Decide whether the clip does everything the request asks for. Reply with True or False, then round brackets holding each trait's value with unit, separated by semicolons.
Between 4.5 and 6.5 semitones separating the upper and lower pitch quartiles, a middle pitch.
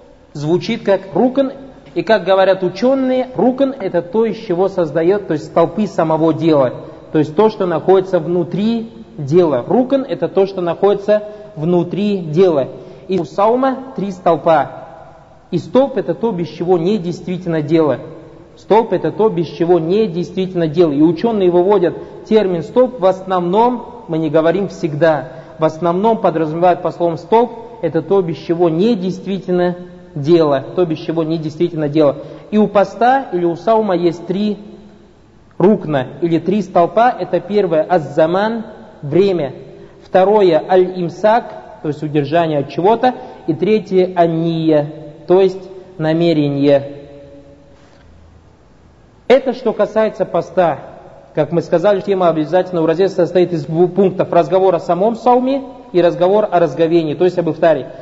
False (3.7 semitones; 180 Hz)